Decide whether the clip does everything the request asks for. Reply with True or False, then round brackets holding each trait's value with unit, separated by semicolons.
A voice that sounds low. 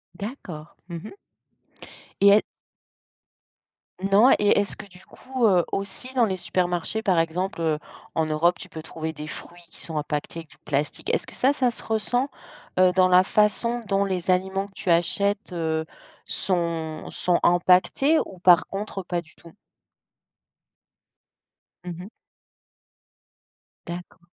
False (180 Hz)